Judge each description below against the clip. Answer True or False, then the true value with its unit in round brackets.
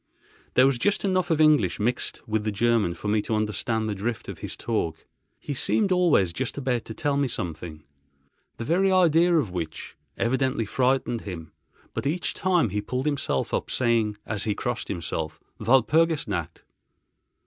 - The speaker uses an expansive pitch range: True (5.9 semitones)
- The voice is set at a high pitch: False (115 Hz)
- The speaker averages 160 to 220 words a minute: True (170 wpm)